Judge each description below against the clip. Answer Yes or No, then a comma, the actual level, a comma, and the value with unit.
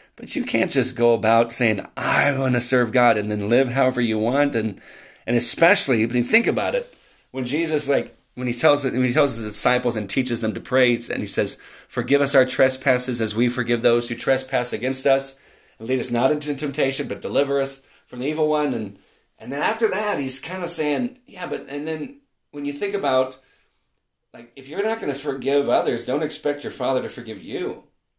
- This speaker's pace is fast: Yes, fast, 215 wpm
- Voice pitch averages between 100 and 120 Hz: No, low, 130 Hz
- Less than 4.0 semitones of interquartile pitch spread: Yes, average, 3.1 semitones